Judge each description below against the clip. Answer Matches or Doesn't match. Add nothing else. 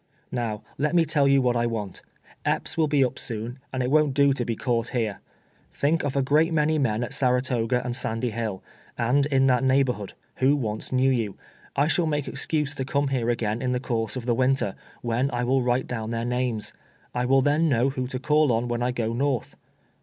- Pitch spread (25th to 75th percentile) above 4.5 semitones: Doesn't match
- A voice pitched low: Matches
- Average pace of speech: Doesn't match